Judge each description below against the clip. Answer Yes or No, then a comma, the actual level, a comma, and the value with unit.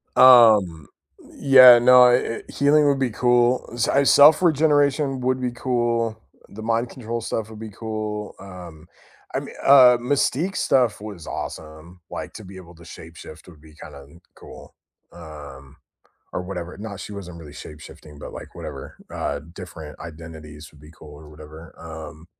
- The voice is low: Yes, low, 105 Hz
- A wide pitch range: Yes, wide, 7.6 semitones